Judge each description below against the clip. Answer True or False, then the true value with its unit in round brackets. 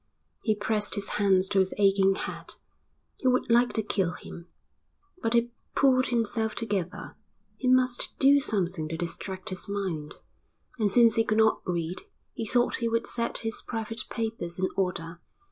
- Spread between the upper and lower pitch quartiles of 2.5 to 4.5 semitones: True (3.8 semitones)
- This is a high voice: True (210 Hz)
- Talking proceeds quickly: False (165 wpm)